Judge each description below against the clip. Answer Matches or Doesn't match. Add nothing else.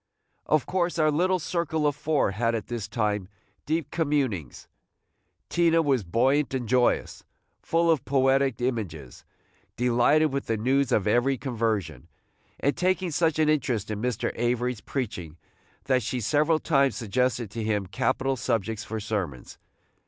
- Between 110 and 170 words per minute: Matches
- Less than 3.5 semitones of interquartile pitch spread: Doesn't match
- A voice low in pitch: Matches